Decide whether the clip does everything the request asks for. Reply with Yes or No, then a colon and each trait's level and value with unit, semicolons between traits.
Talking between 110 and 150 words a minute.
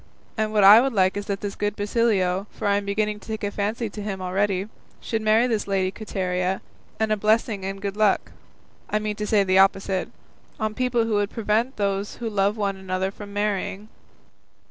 No: average, 200 wpm